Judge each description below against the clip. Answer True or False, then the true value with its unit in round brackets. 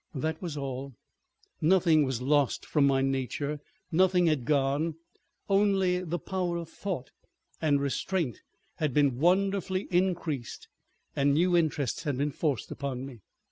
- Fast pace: False (140 wpm)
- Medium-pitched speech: True (150 Hz)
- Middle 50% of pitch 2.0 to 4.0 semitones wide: False (4.4 semitones)